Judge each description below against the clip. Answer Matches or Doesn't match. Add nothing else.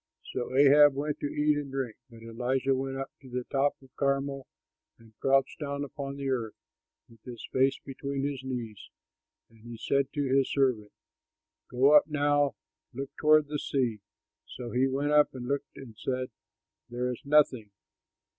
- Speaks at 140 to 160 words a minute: Doesn't match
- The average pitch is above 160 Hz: Doesn't match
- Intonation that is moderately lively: Doesn't match